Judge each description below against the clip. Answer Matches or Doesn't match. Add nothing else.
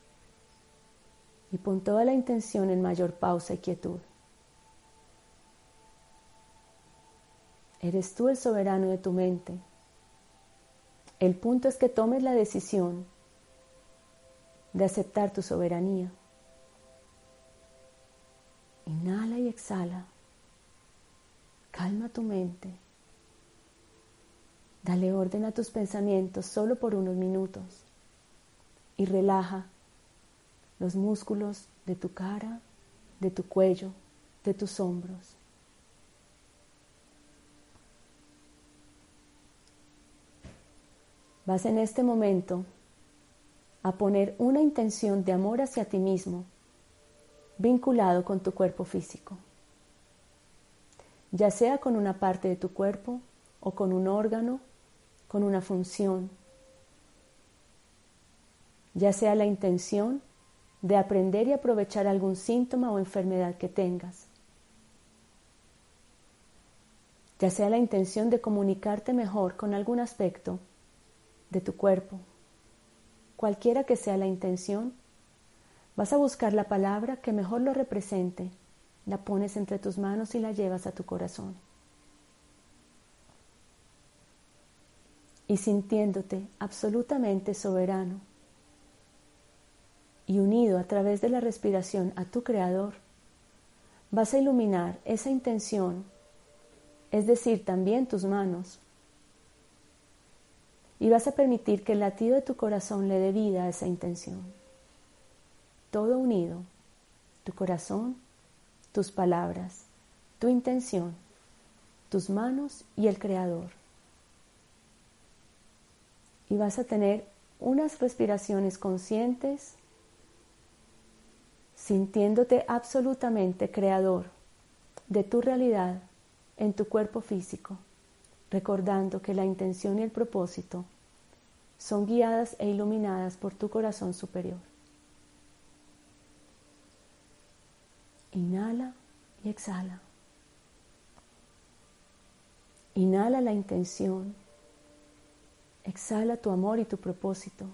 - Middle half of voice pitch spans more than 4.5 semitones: Doesn't match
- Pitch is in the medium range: Doesn't match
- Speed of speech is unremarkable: Doesn't match